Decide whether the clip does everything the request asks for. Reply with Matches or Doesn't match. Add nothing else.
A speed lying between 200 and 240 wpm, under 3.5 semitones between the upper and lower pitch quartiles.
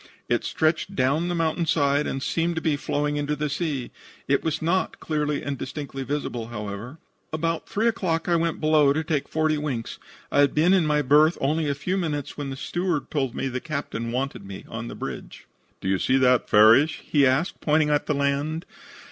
Matches